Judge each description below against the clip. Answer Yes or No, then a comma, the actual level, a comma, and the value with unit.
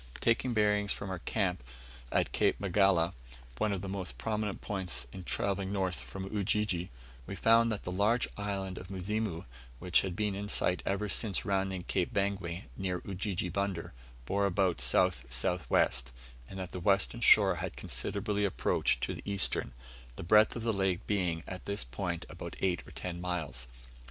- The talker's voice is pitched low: Yes, very low, 95 Hz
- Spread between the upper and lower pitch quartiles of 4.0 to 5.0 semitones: No, narrow, 2.4 semitones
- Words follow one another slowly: No, average, 175 wpm